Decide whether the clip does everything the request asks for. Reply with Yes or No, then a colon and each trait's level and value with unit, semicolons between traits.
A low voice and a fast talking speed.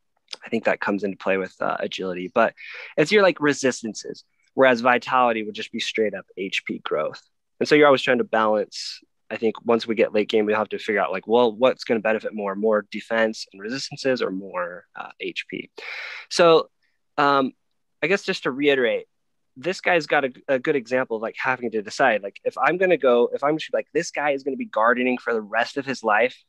Yes: low, 125 Hz; fast, 220 wpm